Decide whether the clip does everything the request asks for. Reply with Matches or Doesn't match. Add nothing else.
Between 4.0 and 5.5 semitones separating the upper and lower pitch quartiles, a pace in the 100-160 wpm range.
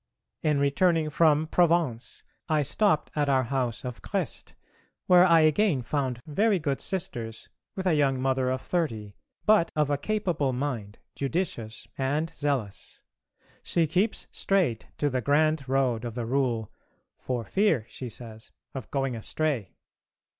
Matches